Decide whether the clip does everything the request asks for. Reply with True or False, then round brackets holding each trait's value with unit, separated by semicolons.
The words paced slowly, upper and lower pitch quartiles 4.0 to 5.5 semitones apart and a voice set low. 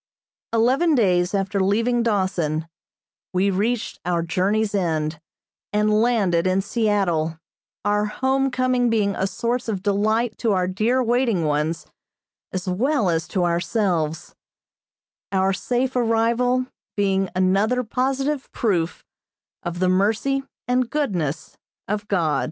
False (125 wpm; 4.7 semitones; 205 Hz)